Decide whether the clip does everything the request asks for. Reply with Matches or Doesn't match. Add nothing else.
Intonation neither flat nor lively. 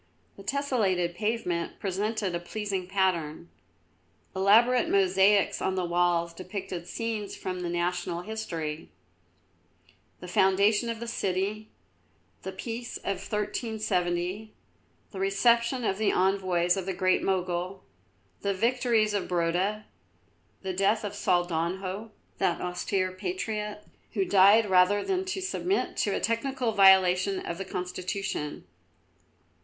Matches